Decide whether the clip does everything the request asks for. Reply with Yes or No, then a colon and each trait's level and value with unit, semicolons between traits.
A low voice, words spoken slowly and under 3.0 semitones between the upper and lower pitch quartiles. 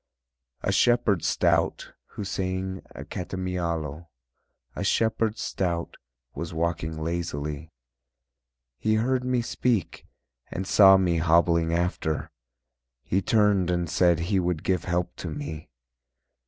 Yes: very low, 90 Hz; slow, 115 wpm; narrow, 2.6 semitones